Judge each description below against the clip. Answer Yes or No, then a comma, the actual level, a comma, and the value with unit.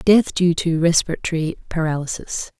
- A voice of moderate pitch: Yes, medium, 165 Hz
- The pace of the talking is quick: No, slow, 115 wpm